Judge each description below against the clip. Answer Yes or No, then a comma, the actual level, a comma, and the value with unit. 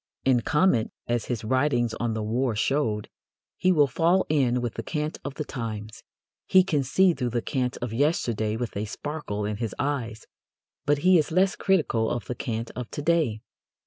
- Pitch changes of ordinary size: Yes, average, 5.0 semitones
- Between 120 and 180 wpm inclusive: No, average, 190 wpm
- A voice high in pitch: No, low, 125 Hz